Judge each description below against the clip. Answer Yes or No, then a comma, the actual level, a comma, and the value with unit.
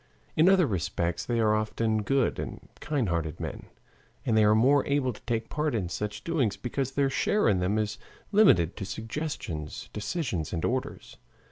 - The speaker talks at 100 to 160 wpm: No, average, 175 wpm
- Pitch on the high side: No, low, 110 Hz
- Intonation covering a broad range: Yes, wide, 5.7 semitones